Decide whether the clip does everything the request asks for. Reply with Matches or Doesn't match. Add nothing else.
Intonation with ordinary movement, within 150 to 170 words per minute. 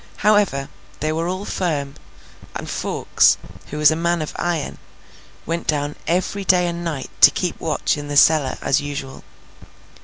Matches